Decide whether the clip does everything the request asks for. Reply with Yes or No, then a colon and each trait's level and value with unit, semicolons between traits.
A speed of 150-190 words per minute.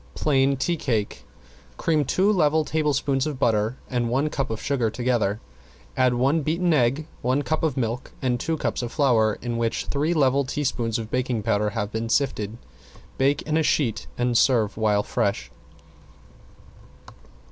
Yes: average, 160 wpm